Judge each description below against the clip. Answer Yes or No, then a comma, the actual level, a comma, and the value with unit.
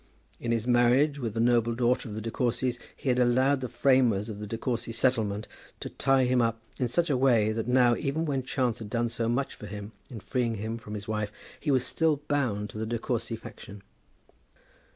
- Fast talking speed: Yes, fast, 220 wpm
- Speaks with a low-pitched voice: Yes, low, 120 Hz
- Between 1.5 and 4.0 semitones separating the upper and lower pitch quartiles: Yes, average, 2.7 semitones